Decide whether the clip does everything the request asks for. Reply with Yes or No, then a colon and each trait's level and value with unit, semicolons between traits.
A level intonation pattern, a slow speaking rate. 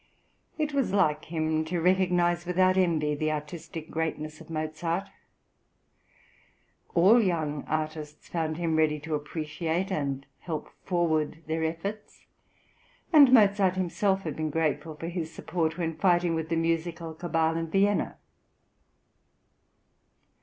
Yes: narrow, 2.3 semitones; slow, 130 wpm